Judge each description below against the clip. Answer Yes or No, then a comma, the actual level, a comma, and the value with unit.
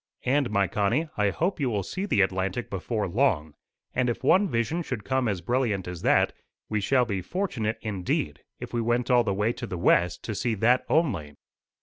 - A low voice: Yes, low, 115 Hz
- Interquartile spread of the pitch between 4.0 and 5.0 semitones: Yes, average, 4.7 semitones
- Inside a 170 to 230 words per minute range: Yes, fast, 205 wpm